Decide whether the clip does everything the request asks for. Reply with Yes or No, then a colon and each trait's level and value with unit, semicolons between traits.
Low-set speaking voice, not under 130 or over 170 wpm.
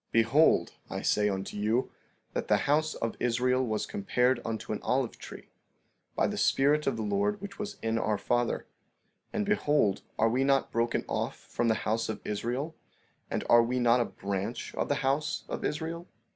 No: low, 120 Hz; average, 185 wpm